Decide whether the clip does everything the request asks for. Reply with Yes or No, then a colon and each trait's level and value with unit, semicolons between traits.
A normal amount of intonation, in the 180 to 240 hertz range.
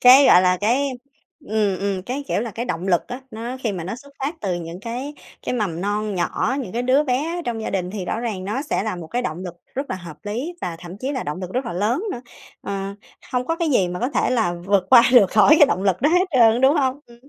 No: wide, 5.7 semitones; high, 225 Hz